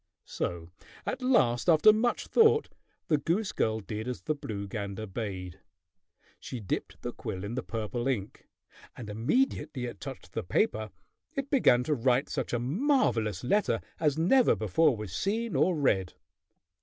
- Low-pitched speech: Yes, low, 125 Hz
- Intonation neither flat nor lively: No, wide, 8.8 semitones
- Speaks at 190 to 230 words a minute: No, average, 155 wpm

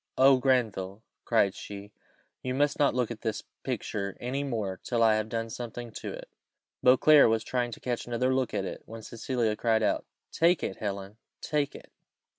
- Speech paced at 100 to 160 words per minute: No, average, 185 wpm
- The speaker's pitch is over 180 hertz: No, low, 115 Hz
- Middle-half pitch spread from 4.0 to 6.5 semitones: No, average, 3.0 semitones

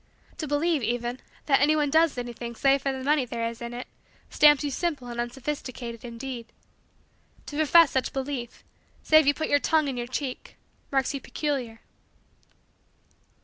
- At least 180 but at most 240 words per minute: No, average, 160 wpm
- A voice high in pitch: Yes, very high, 270 Hz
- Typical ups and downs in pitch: Yes, average, 3.5 semitones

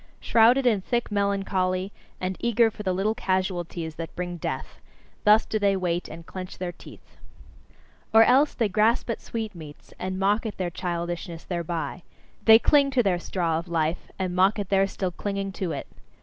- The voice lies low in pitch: No, high, 190 Hz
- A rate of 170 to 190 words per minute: Yes, average, 175 wpm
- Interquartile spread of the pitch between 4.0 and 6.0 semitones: No, average, 3.5 semitones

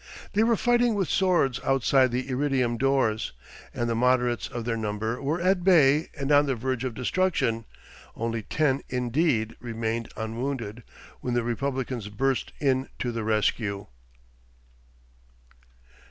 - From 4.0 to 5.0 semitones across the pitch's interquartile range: No, average, 3.5 semitones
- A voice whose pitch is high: No, low, 125 Hz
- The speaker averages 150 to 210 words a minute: No, average, 140 wpm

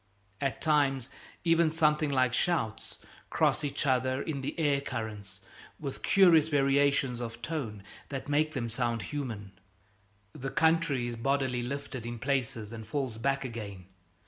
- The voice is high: No, low, 135 Hz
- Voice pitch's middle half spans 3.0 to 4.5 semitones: Yes, average, 3.8 semitones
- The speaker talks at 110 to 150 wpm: Yes, average, 145 wpm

